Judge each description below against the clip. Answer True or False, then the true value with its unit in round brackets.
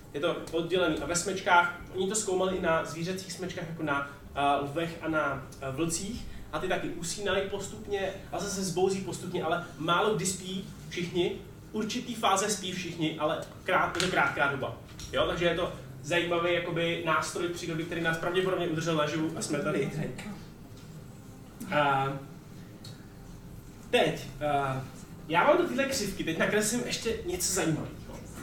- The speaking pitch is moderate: True (170 Hz)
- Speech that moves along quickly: False (150 wpm)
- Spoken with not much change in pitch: False (3.3 semitones)